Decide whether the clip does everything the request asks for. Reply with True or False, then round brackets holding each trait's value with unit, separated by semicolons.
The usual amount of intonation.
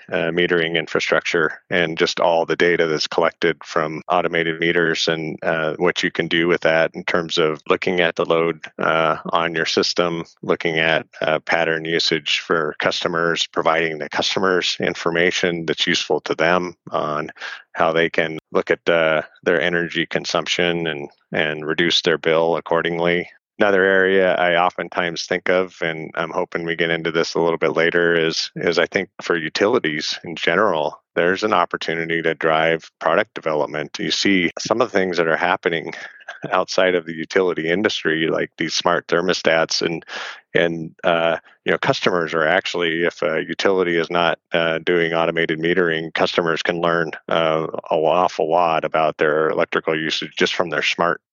False (1.2 semitones)